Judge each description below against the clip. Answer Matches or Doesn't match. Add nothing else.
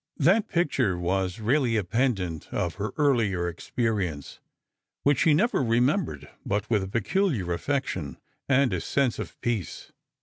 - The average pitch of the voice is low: Matches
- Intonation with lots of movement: Matches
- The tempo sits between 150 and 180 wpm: Doesn't match